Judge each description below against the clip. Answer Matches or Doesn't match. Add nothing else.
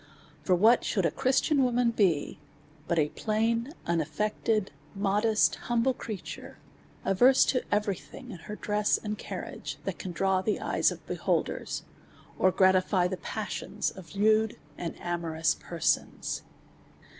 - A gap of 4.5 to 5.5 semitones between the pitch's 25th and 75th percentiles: Doesn't match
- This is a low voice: Doesn't match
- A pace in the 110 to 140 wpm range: Matches